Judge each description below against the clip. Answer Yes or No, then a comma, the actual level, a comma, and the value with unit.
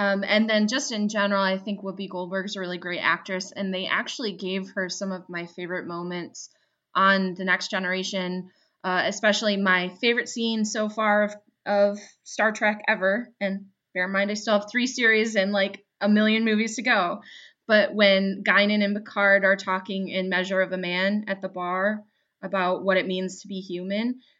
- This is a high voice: Yes, high, 195 Hz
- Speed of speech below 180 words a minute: No, average, 195 wpm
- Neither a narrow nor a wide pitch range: No, narrow, 2.1 semitones